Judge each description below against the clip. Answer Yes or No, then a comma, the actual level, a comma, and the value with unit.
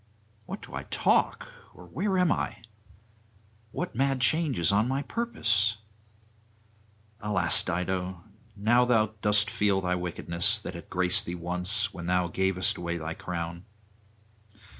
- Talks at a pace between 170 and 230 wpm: No, average, 140 wpm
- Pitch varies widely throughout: No, average, 4.1 semitones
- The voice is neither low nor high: No, very low, 95 Hz